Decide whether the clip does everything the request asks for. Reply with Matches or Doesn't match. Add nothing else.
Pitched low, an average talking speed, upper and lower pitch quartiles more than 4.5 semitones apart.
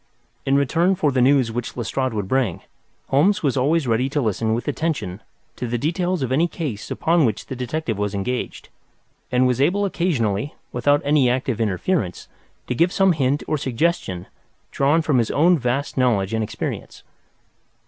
Matches